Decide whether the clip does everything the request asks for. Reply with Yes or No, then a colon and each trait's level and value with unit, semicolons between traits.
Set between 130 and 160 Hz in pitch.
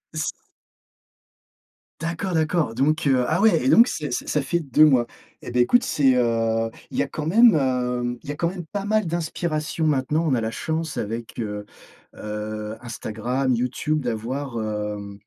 Yes: low, 135 Hz